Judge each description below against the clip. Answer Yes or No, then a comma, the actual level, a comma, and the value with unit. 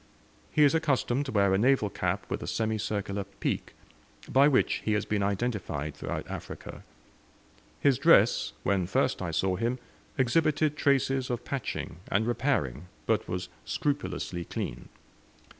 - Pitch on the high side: No, low, 110 Hz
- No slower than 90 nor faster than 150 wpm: Yes, average, 140 wpm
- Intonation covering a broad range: Yes, wide, 5.9 semitones